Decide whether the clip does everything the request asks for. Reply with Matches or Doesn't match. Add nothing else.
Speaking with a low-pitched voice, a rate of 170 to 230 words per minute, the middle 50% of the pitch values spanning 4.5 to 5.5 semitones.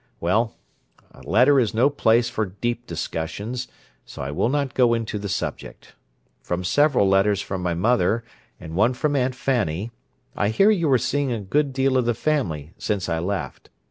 Matches